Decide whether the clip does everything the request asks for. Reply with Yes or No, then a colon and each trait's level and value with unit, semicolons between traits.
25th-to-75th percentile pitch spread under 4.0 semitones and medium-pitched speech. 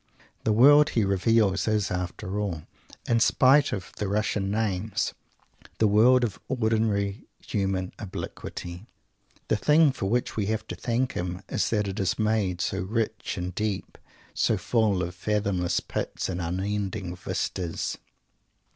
No: average, 3.0 semitones; low, 105 Hz